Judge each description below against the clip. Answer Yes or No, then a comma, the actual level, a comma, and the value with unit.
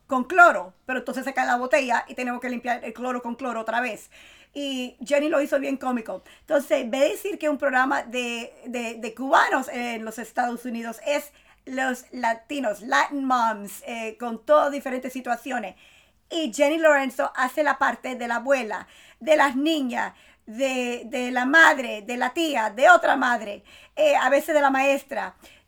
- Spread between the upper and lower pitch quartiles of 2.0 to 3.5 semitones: Yes, average, 3.1 semitones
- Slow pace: No, average, 180 wpm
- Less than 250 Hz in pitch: No, very high, 260 Hz